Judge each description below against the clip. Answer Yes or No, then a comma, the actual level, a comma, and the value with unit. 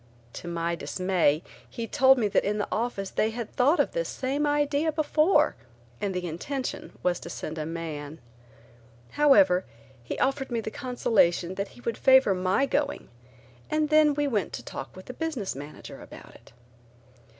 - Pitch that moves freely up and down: Yes, wide, 8.0 semitones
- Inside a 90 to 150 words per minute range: No, average, 170 wpm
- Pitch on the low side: No, high, 230 Hz